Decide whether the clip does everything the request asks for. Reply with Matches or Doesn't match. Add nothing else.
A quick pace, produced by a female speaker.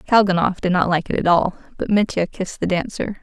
Matches